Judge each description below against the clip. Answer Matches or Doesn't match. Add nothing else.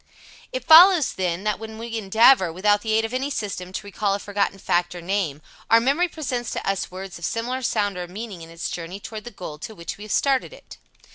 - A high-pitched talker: Matches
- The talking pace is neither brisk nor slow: Doesn't match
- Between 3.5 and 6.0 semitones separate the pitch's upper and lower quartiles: Matches